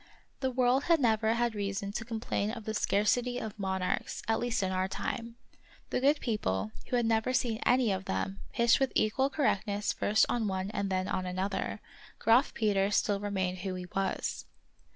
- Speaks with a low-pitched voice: No, high, 215 Hz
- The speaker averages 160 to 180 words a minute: No, average, 190 wpm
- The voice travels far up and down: No, average, 3.7 semitones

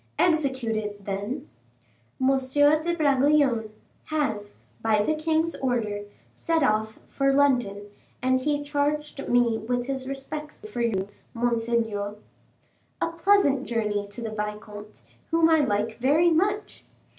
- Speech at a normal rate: No, slow, 125 wpm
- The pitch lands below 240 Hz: No, very high, 260 Hz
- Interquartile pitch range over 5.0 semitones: Yes, wide, 5.5 semitones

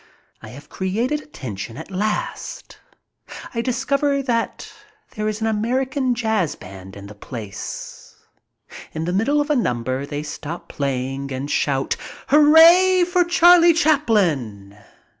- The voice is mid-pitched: No, high, 210 Hz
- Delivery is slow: Yes, slow, 130 wpm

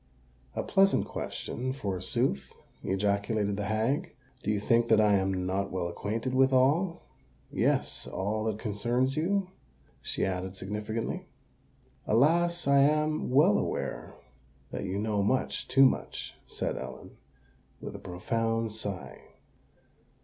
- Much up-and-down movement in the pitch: No, average, 5.0 semitones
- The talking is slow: Yes, slow, 120 wpm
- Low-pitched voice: Yes, low, 110 Hz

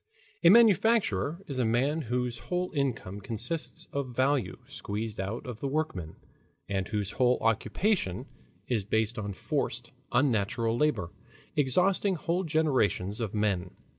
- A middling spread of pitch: No, wide, 6.6 semitones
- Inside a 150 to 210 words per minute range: No, slow, 135 wpm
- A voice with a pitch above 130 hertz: No, low, 120 Hz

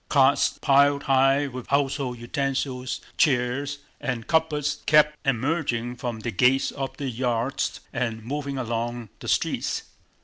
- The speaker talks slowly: Yes, slow, 130 wpm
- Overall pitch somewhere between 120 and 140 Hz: Yes, low, 135 Hz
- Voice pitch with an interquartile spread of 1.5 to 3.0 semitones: Yes, average, 2.7 semitones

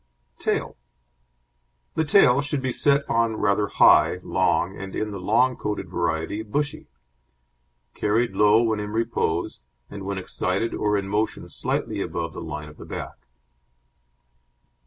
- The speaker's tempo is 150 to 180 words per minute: No, average, 140 wpm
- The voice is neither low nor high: No, low, 105 Hz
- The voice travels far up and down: No, average, 3.2 semitones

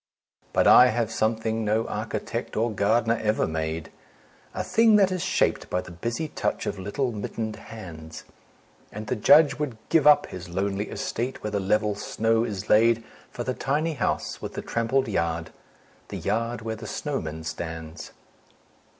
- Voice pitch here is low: Yes, low, 110 Hz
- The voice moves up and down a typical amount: Yes, average, 4.0 semitones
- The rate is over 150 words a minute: Yes, average, 165 wpm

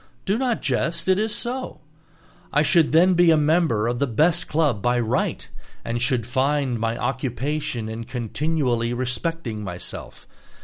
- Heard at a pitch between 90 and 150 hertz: Yes, low, 135 Hz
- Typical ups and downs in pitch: No, wide, 5.7 semitones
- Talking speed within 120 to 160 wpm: Yes, average, 150 wpm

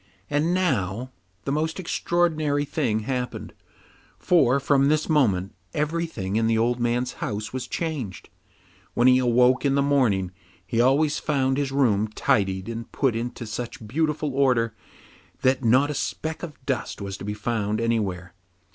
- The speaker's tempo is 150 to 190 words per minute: Yes, average, 155 wpm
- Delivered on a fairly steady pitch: No, average, 4.6 semitones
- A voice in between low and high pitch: No, low, 125 Hz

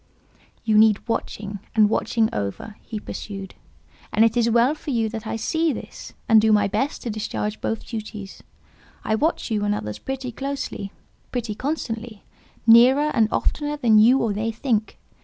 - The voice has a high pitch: Yes, high, 225 Hz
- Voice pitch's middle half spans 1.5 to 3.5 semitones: Yes, average, 2.7 semitones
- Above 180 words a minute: No, average, 170 wpm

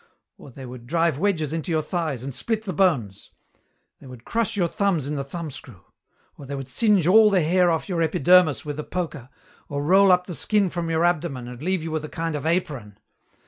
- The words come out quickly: Yes, fast, 220 wpm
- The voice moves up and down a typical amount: Yes, average, 4.7 semitones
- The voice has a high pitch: No, medium, 160 Hz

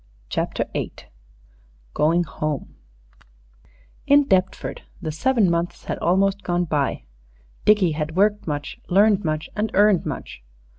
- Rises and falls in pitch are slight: No, average, 4.7 semitones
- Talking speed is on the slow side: Yes, slow, 120 wpm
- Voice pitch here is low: No, medium, 180 Hz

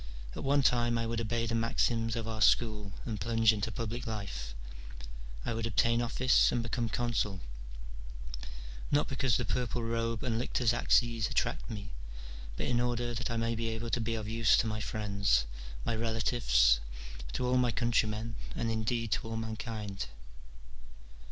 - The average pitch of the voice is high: No, low, 115 Hz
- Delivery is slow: No, average, 165 wpm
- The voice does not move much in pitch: Yes, narrow, 1.5 semitones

